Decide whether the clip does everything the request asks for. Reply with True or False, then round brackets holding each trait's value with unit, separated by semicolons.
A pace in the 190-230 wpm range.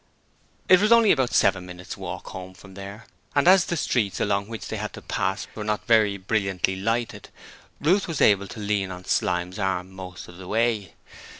True (195 wpm)